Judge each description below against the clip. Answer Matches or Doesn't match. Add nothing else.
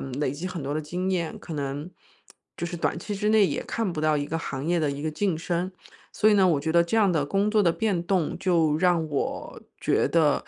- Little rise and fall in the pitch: Doesn't match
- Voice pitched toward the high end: Doesn't match